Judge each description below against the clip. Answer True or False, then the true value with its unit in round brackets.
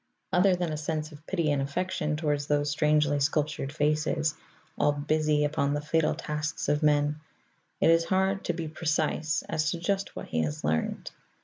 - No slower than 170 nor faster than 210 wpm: True (180 wpm)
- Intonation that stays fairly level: True (1.7 semitones)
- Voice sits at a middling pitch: True (150 Hz)